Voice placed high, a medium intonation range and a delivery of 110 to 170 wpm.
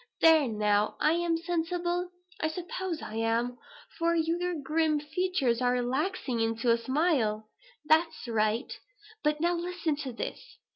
No: very high, 305 Hz; wide, 6.3 semitones; average, 140 wpm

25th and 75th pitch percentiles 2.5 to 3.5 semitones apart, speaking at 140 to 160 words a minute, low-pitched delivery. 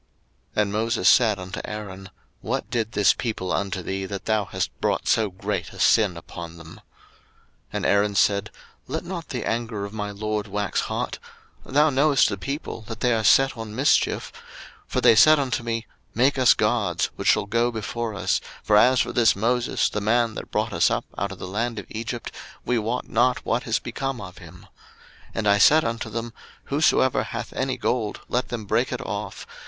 No: average, 3.1 semitones; average, 200 wpm; low, 110 Hz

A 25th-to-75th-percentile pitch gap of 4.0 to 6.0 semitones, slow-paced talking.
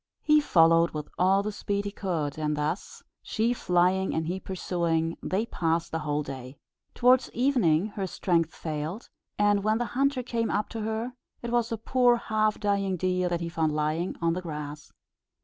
No: average, 5.1 semitones; average, 185 wpm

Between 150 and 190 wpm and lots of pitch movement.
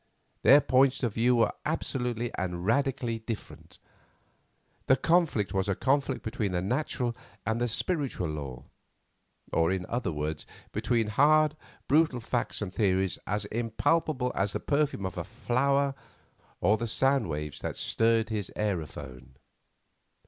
No: average, 140 wpm; wide, 5.8 semitones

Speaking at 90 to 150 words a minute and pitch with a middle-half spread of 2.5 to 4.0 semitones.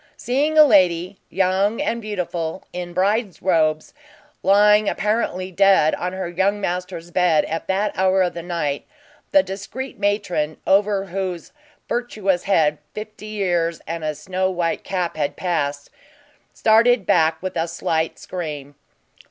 Yes: average, 140 wpm; average, 3.3 semitones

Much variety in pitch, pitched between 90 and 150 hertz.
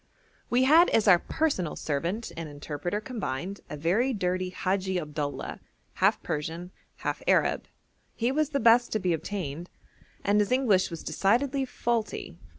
No: wide, 6.1 semitones; high, 195 Hz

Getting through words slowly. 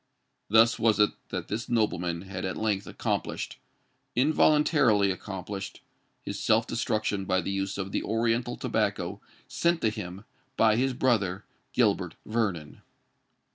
Yes: slow, 125 wpm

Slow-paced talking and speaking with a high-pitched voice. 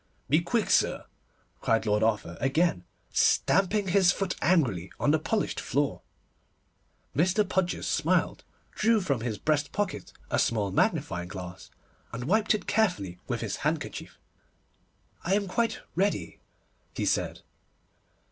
No: slow, 130 wpm; medium, 160 Hz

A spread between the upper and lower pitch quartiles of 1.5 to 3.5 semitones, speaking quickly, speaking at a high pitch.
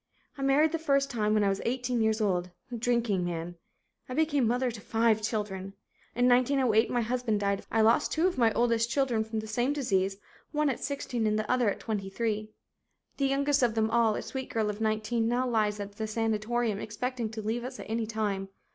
Yes: average, 2.9 semitones; fast, 215 wpm; high, 225 Hz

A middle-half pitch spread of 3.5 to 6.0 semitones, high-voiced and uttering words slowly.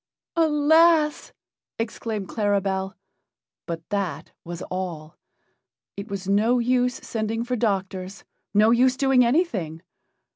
Yes: average, 4.7 semitones; high, 215 Hz; slow, 105 wpm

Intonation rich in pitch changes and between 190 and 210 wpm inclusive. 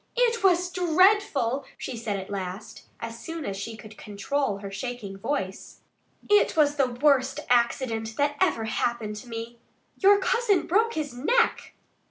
No: wide, 7.8 semitones; average, 155 wpm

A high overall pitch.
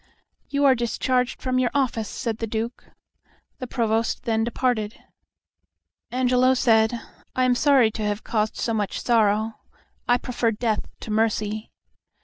Yes: high, 230 Hz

